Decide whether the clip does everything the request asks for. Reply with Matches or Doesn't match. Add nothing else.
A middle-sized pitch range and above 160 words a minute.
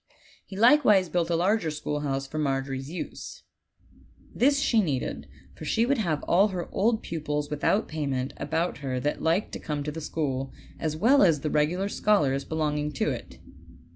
Matches